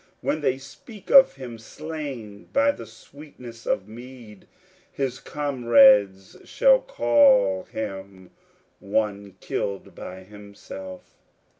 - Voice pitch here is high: No, low, 115 Hz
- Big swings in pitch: Yes, wide, 6.7 semitones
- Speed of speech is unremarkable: No, slow, 105 wpm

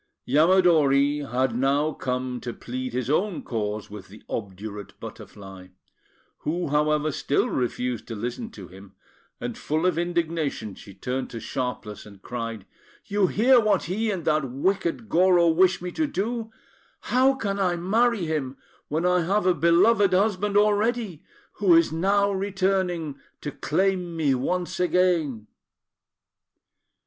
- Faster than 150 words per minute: No, average, 140 wpm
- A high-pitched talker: No, medium, 165 Hz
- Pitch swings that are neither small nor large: No, wide, 6.9 semitones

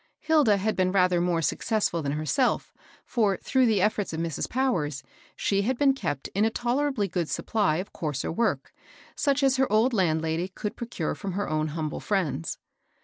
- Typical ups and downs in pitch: No, wide, 6.3 semitones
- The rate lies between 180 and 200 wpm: Yes, average, 185 wpm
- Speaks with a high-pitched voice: Yes, high, 195 Hz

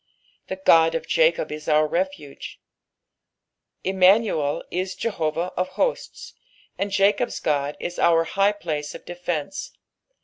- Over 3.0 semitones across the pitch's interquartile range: Yes, average, 4.2 semitones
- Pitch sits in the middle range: Yes, medium, 180 Hz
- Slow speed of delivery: Yes, slow, 130 wpm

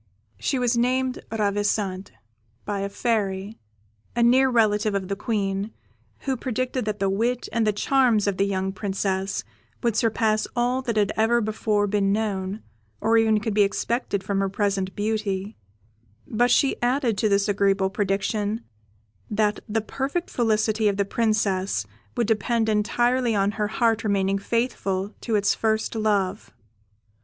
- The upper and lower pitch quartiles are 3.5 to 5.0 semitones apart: No, average, 2.7 semitones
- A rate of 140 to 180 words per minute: Yes, average, 150 wpm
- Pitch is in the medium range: No, high, 215 Hz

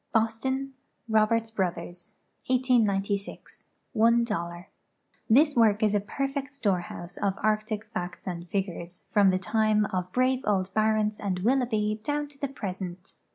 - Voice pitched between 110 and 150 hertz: No, high, 215 Hz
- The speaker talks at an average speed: No, slow, 130 wpm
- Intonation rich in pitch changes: No, average, 3.7 semitones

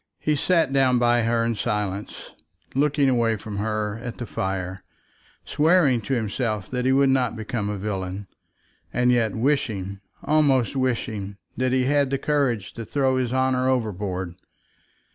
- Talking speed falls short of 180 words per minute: Yes, average, 155 wpm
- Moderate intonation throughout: Yes, average, 4.1 semitones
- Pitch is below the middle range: Yes, low, 120 Hz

